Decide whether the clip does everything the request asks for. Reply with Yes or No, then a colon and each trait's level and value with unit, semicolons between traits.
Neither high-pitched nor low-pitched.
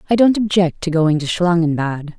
Yes: medium, 175 Hz